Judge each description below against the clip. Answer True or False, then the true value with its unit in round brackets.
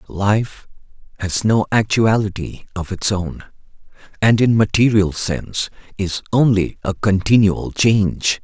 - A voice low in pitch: True (100 Hz)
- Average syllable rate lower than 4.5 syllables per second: True (4.0 syllables/s)